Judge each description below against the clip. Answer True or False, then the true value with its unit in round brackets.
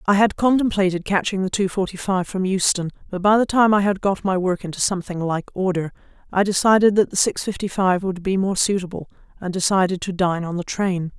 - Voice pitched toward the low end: False (190 Hz)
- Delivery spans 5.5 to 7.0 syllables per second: True (5.7 syllables/s)